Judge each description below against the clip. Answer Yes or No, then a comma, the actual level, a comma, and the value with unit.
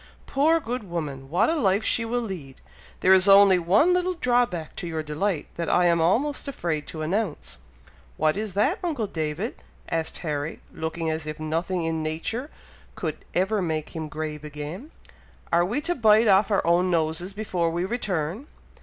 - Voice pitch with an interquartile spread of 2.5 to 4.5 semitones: No, wide, 5.6 semitones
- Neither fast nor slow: Yes, average, 175 wpm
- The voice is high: No, medium, 180 Hz